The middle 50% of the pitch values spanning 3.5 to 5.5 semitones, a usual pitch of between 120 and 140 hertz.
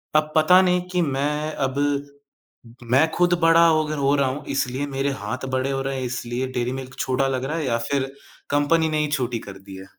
No: average, 2.9 semitones; low, 135 Hz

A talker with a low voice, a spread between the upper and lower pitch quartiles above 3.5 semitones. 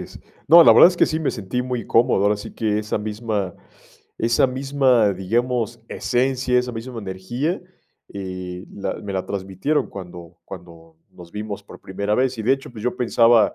Yes: low, 110 Hz; average, 4.5 semitones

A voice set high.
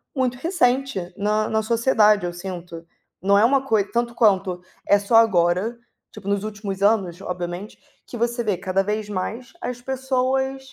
Yes: high, 215 Hz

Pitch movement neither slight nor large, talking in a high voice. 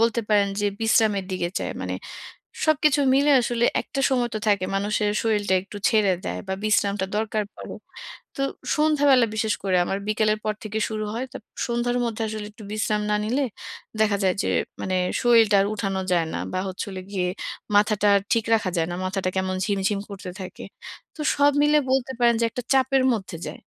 Yes: average, 3.3 semitones; high, 215 Hz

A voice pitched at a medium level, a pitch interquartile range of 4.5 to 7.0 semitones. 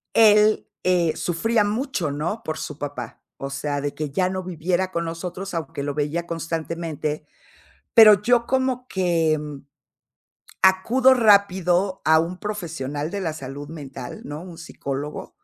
Yes: medium, 170 Hz; average, 4.9 semitones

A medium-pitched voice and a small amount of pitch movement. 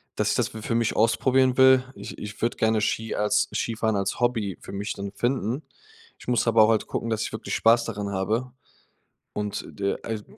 No: low, 110 Hz; narrow, 2.3 semitones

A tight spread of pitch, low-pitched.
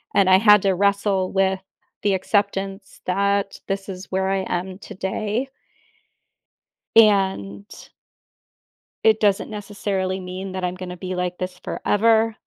No: narrow, 1.5 semitones; high, 195 Hz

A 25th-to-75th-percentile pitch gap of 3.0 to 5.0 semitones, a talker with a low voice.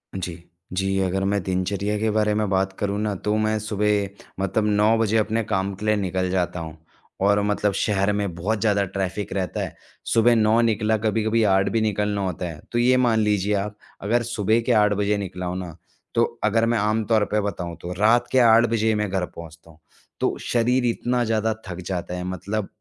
No: narrow, 2.5 semitones; low, 105 Hz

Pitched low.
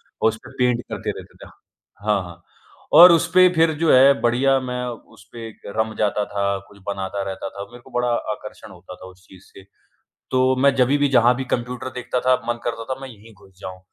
Yes: low, 120 Hz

